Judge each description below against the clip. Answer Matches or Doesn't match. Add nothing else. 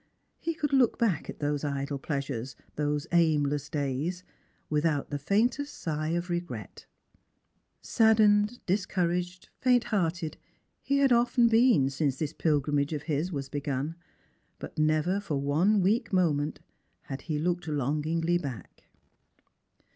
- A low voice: Doesn't match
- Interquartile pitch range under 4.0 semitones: Doesn't match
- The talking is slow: Matches